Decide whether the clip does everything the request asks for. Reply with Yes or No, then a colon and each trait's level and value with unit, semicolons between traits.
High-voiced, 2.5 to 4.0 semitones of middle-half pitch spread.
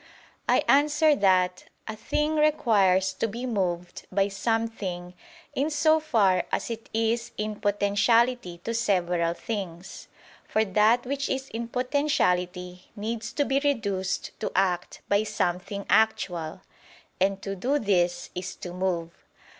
No: high, 205 Hz; average, 4.6 semitones